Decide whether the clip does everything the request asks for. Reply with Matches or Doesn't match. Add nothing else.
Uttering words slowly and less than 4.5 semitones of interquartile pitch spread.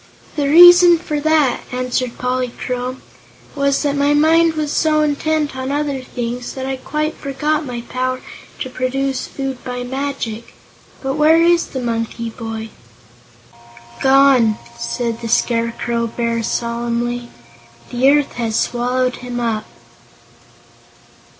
Matches